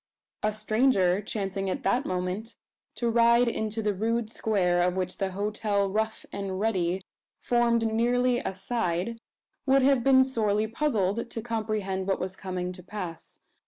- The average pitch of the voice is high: Yes, high, 215 Hz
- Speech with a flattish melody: No, average, 3.6 semitones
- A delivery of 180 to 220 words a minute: No, average, 155 wpm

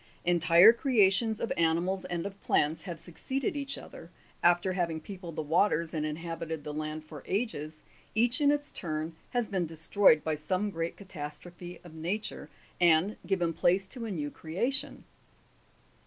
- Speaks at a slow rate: No, average, 160 wpm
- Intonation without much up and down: No, average, 4.0 semitones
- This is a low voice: No, medium, 175 Hz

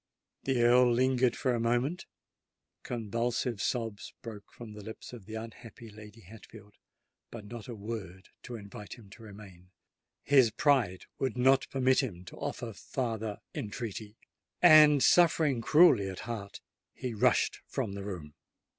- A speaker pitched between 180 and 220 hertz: No, low, 115 Hz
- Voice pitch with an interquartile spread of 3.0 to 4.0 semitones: Yes, average, 3.5 semitones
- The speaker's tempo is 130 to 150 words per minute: Yes, average, 140 wpm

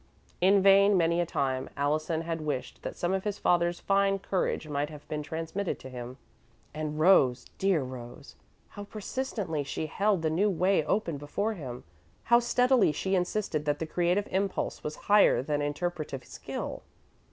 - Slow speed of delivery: No, average, 165 wpm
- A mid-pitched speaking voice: Yes, medium, 170 Hz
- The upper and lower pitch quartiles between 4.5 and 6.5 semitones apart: Yes, average, 4.9 semitones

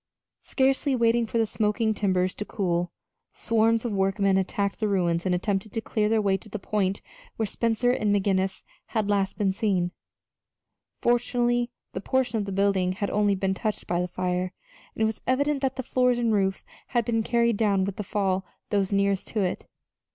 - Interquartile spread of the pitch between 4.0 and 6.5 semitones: No, average, 3.1 semitones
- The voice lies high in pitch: Yes, high, 205 Hz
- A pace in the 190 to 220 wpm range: Yes, average, 195 wpm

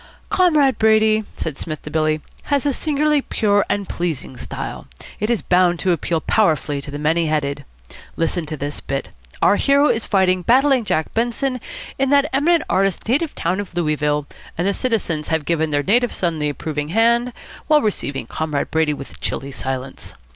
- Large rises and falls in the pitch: Yes, wide, 7.7 semitones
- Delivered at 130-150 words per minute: No, average, 175 wpm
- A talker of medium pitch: Yes, medium, 180 Hz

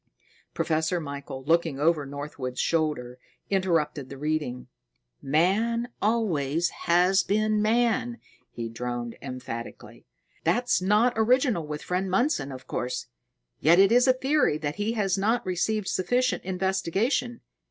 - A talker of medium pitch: Yes, medium, 180 Hz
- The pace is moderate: No, slow, 120 wpm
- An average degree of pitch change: No, wide, 7.2 semitones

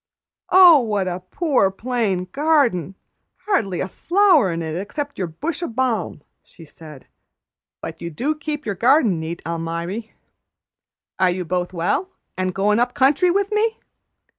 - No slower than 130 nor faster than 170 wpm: Yes, average, 150 wpm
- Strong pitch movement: Yes, wide, 8.8 semitones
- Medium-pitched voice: No, high, 210 Hz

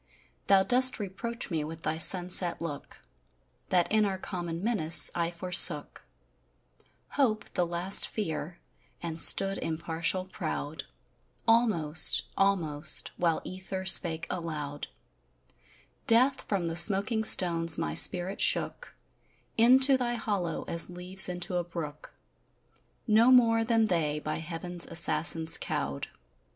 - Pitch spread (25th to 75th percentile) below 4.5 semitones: Yes, average, 4.1 semitones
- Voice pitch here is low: No, medium, 180 Hz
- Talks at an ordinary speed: No, slow, 120 wpm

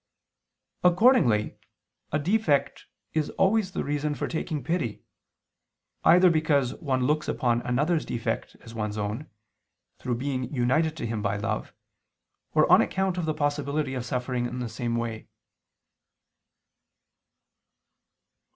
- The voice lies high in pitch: No, medium, 140 Hz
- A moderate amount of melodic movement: Yes, average, 4.8 semitones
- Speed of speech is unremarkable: No, slow, 125 wpm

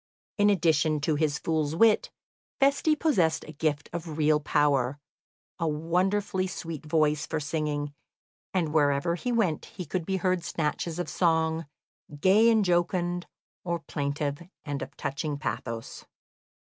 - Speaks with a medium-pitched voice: Yes, medium, 160 Hz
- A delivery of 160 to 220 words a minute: No, slow, 135 wpm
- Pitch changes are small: No, average, 3.3 semitones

